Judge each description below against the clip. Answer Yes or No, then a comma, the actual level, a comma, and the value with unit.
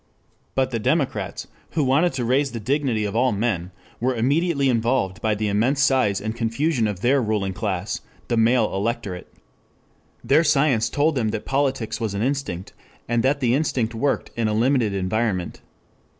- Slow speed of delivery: No, average, 170 wpm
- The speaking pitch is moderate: No, low, 120 Hz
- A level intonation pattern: No, average, 4.1 semitones